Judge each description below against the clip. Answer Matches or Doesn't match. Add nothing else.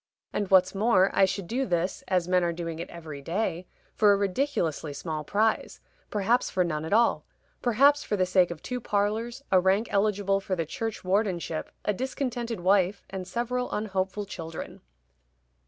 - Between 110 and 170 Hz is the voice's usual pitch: Doesn't match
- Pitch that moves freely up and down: Doesn't match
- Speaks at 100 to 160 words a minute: Doesn't match